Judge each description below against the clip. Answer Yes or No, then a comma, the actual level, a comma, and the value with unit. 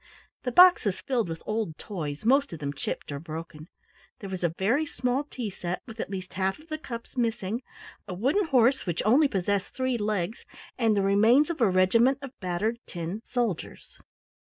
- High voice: Yes, high, 215 Hz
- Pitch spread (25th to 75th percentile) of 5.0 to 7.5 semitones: Yes, wide, 5.6 semitones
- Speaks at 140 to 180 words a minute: No, average, 190 wpm